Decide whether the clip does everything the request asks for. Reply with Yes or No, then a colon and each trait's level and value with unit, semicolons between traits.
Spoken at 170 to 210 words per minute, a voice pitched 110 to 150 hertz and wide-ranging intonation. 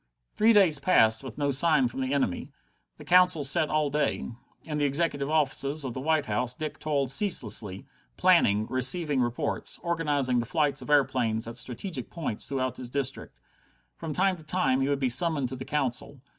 No: average, 185 wpm; medium, 140 Hz; average, 3.4 semitones